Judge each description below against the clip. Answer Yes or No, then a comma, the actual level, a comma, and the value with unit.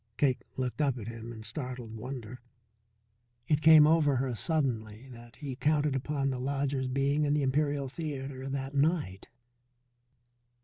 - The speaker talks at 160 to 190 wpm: No, average, 145 wpm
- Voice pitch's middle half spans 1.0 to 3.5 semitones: Yes, average, 2.7 semitones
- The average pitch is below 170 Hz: Yes, low, 135 Hz